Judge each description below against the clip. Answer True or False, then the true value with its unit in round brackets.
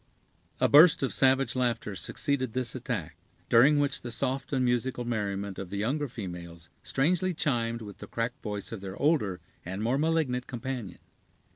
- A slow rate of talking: False (165 wpm)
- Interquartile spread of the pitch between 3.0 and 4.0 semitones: False (4.8 semitones)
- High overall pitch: False (120 Hz)